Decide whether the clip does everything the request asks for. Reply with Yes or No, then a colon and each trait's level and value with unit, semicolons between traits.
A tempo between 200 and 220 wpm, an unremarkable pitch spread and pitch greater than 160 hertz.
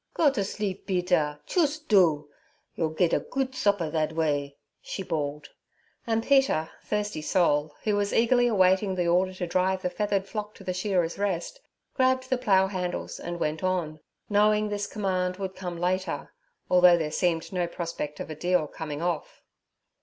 No: average, 170 wpm; average, 3.9 semitones; medium, 185 Hz